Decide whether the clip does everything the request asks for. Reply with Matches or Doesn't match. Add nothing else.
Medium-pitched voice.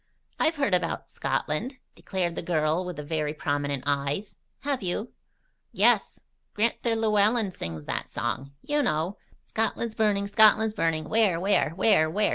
Doesn't match